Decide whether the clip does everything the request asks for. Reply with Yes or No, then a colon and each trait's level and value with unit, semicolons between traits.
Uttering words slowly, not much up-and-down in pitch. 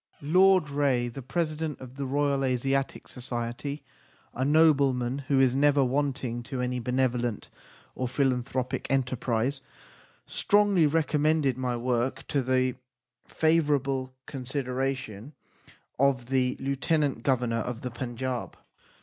Yes: slow, 120 wpm; narrow, 2.2 semitones